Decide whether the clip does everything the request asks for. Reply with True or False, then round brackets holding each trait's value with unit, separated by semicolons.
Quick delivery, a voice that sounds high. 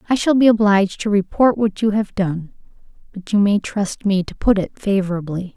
False (195 wpm; 200 Hz)